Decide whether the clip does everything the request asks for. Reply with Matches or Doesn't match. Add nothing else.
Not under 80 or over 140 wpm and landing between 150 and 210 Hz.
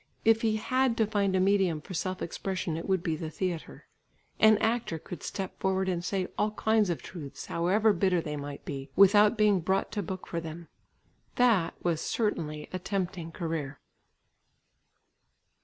Doesn't match